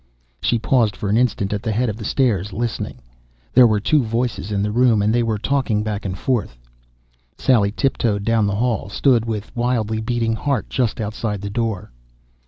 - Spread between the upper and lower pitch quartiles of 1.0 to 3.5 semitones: Yes, average, 2.7 semitones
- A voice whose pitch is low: Yes, low, 110 Hz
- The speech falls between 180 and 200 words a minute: Yes, average, 190 wpm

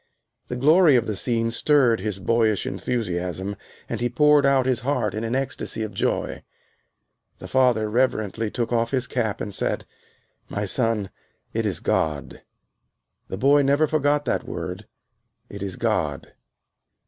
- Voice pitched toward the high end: No, low, 115 Hz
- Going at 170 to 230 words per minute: No, average, 150 wpm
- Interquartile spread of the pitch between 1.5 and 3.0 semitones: No, average, 4.1 semitones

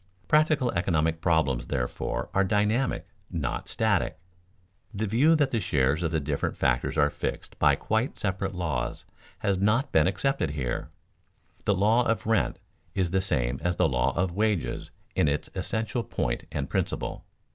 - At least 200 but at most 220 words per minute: No, average, 155 wpm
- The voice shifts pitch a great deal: Yes, wide, 6.8 semitones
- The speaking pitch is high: No, very low, 95 Hz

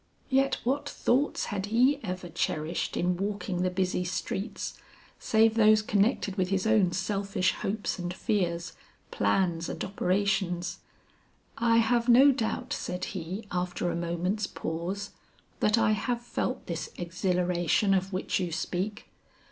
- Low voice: No, high, 190 Hz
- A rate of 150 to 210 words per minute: No, average, 140 wpm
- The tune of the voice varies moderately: Yes, average, 3.6 semitones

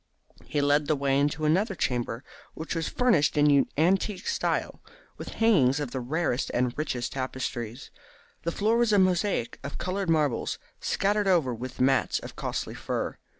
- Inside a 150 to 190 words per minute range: Yes, average, 160 wpm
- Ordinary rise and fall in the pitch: No, wide, 6.1 semitones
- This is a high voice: No, medium, 150 Hz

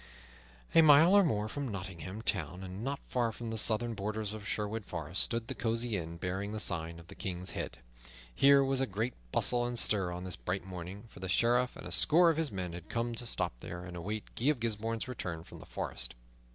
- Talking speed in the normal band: No, fast, 225 wpm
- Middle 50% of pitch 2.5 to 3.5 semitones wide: No, average, 4.9 semitones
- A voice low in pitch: Yes, low, 110 Hz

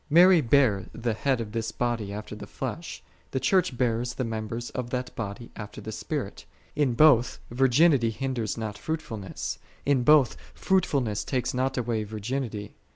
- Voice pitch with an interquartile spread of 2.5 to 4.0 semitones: Yes, average, 3.4 semitones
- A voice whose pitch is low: Yes, low, 120 Hz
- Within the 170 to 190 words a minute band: No, average, 160 wpm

